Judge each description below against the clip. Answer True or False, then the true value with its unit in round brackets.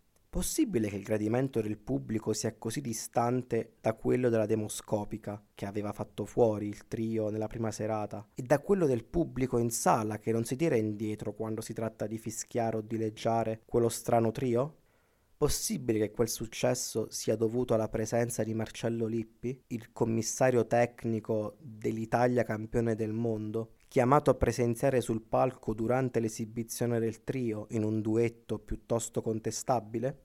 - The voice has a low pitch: True (115 Hz)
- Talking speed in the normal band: True (155 wpm)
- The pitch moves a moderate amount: False (1.5 semitones)